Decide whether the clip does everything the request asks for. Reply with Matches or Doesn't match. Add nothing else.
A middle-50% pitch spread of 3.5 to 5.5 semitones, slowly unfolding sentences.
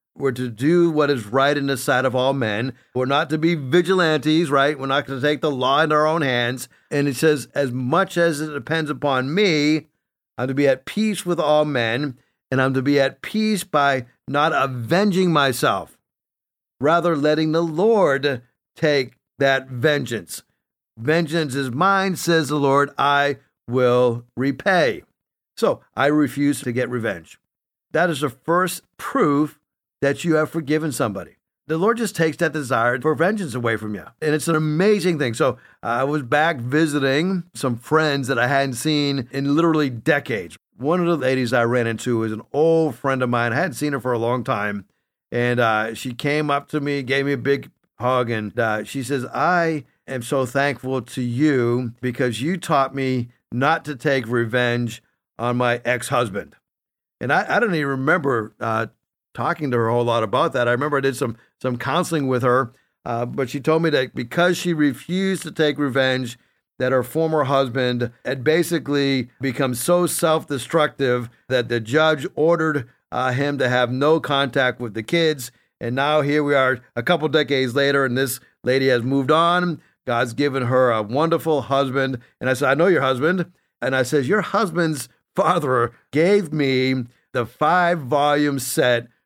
Doesn't match